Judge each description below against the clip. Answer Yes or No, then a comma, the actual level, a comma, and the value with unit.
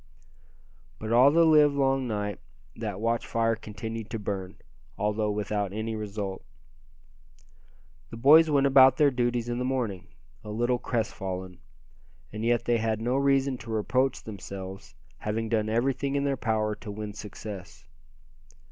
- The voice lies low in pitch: Yes, low, 115 Hz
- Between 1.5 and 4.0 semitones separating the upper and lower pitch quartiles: Yes, average, 3.6 semitones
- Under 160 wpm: Yes, average, 145 wpm